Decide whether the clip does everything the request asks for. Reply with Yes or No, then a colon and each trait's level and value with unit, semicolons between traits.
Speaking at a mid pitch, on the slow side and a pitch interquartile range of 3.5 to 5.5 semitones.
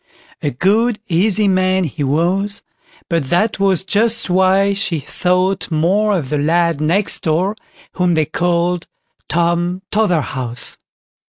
No: medium, 180 Hz; slow, 125 wpm; average, 3.1 semitones